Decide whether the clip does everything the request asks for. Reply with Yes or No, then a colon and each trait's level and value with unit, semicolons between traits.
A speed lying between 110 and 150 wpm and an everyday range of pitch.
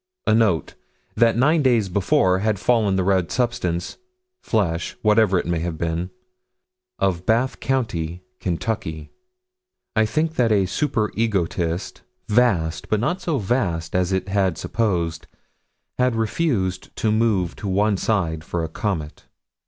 Yes: average, 140 wpm; average, 4.7 semitones